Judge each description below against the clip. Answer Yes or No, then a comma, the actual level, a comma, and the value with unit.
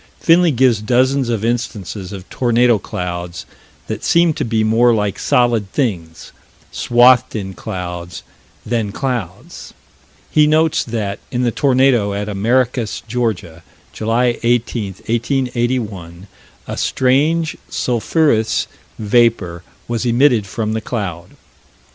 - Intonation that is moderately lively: Yes, average, 3.8 semitones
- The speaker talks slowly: Yes, slow, 115 wpm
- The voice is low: Yes, low, 115 Hz